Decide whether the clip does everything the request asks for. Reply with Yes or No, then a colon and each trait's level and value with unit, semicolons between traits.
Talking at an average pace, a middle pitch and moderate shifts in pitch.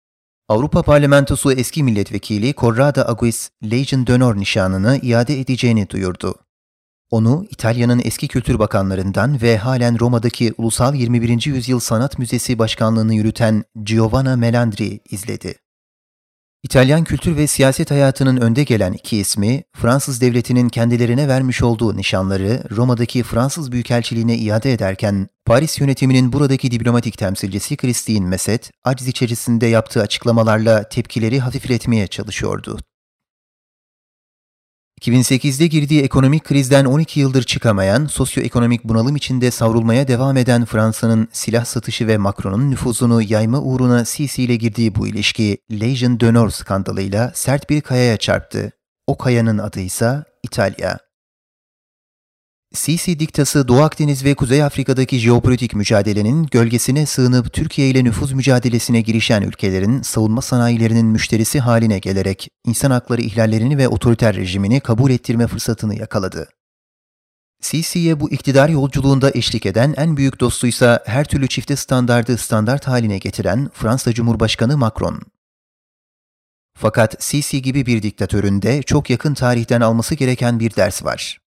No: average, 120 wpm; low, 120 Hz; average, 3.1 semitones